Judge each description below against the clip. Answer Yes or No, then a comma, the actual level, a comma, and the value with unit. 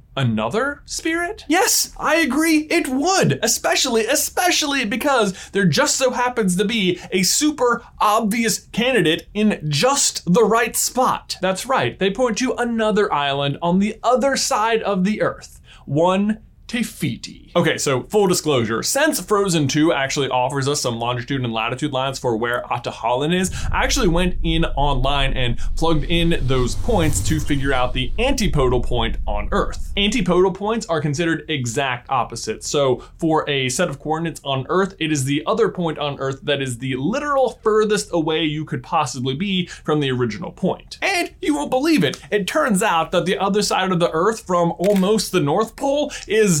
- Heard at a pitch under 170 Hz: No, medium, 185 Hz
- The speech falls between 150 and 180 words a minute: Yes, average, 170 wpm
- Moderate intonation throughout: No, wide, 7.6 semitones